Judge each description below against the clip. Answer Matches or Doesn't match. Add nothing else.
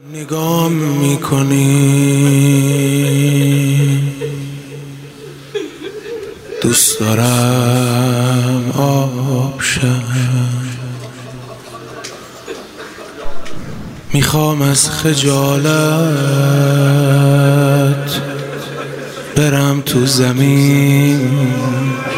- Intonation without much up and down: Matches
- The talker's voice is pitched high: Doesn't match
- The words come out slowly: Matches